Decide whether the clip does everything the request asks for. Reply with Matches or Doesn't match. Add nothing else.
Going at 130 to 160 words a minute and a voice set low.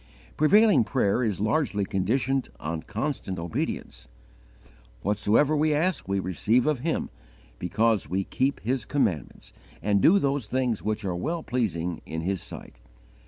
Matches